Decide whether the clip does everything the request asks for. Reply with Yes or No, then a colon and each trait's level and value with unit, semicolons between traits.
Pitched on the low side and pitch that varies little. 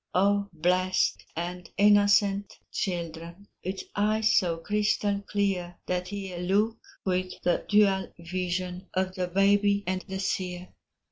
No: medium, 185 Hz; narrow, 2.2 semitones